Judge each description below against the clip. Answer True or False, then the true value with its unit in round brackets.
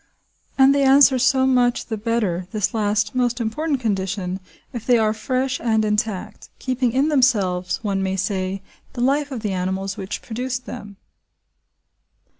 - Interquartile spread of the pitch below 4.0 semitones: False (4.7 semitones)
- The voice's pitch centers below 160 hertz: False (225 Hz)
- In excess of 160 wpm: False (155 wpm)